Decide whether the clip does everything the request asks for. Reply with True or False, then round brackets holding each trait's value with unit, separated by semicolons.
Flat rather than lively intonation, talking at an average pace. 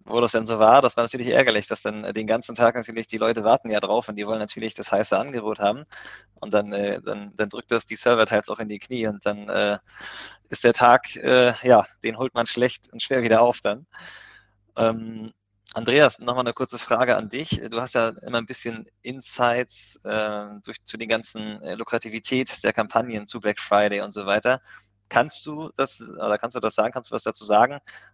False (2.3 semitones; 215 wpm)